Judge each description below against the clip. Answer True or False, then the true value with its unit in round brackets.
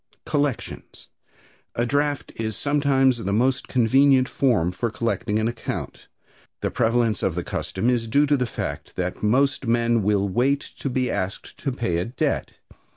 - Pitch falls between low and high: False (120 Hz)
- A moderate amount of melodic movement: True (3.9 semitones)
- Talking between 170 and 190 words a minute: False (160 wpm)